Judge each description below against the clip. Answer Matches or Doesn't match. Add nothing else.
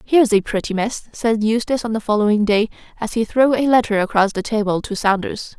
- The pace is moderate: Doesn't match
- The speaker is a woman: Matches